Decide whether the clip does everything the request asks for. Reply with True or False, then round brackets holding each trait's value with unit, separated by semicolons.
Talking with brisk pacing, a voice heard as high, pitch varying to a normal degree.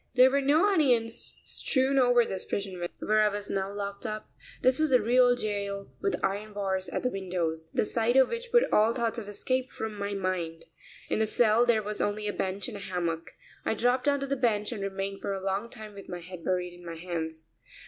True (220 wpm; 210 Hz; 4.3 semitones)